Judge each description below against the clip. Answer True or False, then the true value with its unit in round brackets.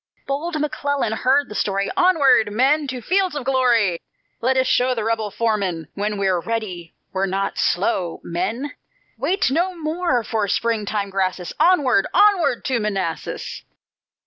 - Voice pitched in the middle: False (230 Hz)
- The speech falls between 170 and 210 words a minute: False (145 wpm)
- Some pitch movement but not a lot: False (6.2 semitones)